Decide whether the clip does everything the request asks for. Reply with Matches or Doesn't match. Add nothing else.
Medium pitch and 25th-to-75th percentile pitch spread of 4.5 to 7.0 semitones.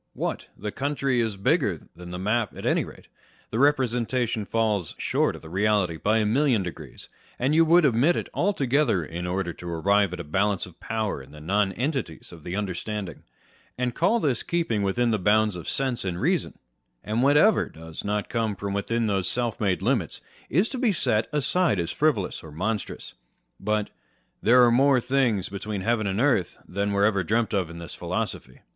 Doesn't match